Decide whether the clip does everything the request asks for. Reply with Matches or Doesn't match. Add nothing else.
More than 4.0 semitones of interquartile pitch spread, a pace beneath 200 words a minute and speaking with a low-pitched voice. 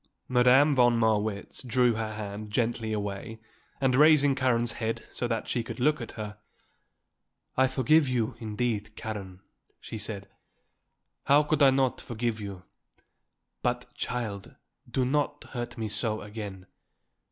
Doesn't match